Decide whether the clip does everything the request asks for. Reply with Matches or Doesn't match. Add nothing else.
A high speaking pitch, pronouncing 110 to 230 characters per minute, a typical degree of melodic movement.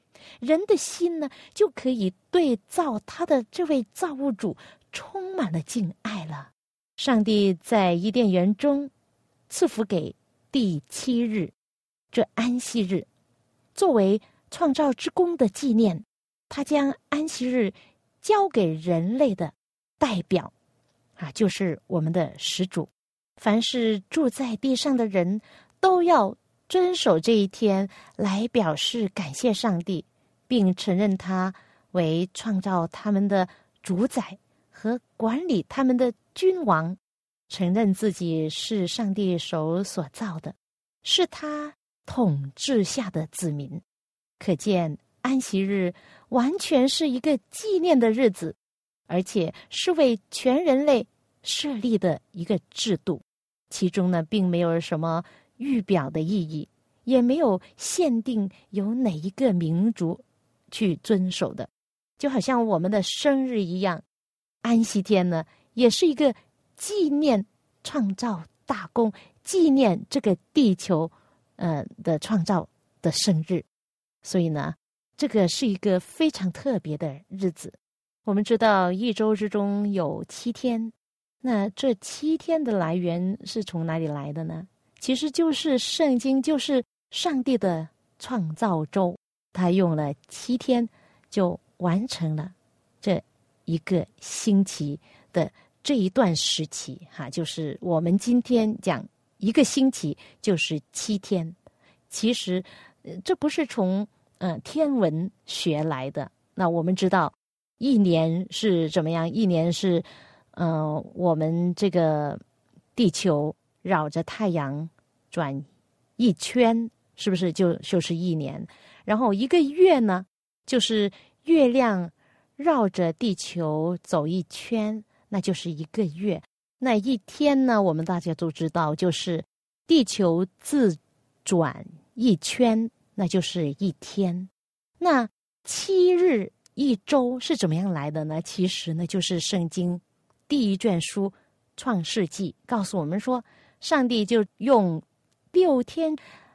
Doesn't match